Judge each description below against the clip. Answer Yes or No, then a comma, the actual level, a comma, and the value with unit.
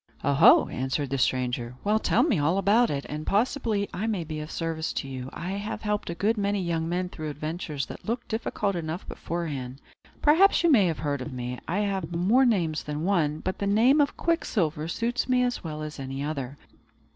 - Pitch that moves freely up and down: Yes, wide, 5.9 semitones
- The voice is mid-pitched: Yes, medium, 170 Hz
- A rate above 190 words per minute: Yes, fast, 205 wpm